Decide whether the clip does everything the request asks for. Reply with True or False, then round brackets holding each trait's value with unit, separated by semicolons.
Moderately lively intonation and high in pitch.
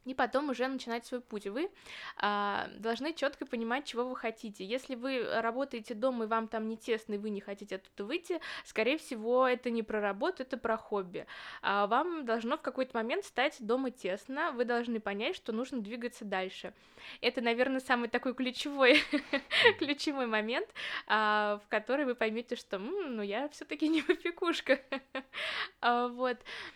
True (3.3 semitones; 245 Hz)